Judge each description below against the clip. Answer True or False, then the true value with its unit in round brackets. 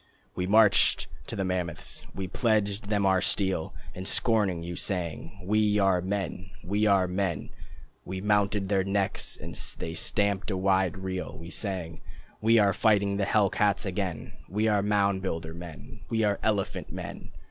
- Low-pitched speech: True (95 Hz)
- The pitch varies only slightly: True (2.0 semitones)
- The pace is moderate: True (165 wpm)